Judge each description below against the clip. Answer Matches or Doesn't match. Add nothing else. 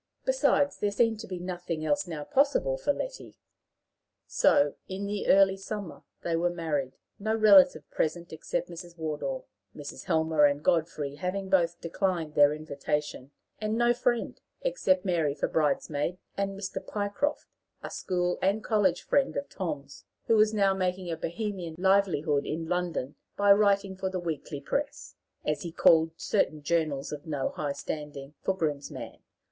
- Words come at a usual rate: Matches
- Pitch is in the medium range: Matches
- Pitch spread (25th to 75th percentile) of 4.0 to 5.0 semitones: Matches